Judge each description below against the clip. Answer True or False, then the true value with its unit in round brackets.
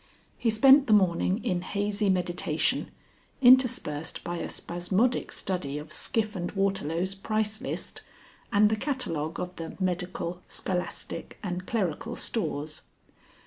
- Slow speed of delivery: True (125 wpm)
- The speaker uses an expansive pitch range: False (3.8 semitones)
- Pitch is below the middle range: False (190 Hz)